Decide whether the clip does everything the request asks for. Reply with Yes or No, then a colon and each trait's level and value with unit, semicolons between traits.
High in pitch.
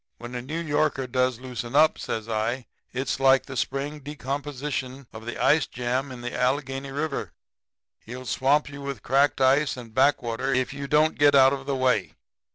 No: low, 135 Hz